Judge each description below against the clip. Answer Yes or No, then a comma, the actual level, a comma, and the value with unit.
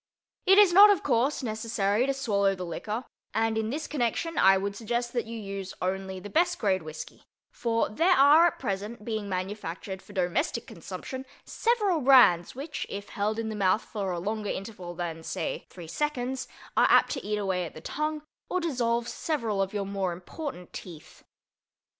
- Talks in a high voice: Yes, high, 215 Hz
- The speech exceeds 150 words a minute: Yes, average, 180 wpm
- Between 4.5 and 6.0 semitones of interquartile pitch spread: Yes, wide, 5.6 semitones